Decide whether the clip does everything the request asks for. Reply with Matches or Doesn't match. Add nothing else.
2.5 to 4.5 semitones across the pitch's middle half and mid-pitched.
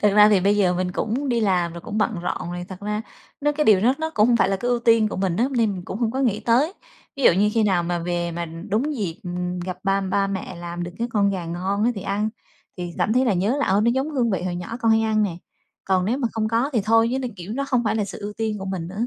Doesn't match